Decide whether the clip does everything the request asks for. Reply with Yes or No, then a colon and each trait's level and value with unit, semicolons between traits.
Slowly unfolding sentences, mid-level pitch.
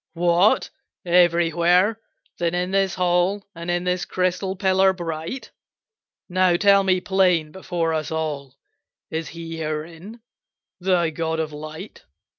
Yes: slow, 125 wpm; medium, 175 Hz